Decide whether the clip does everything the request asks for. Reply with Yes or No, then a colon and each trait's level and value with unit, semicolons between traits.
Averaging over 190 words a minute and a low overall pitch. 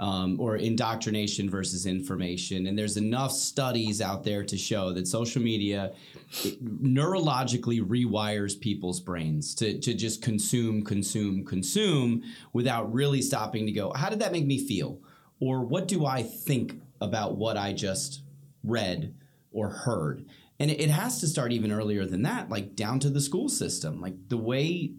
No: average, 160 wpm; low, 115 Hz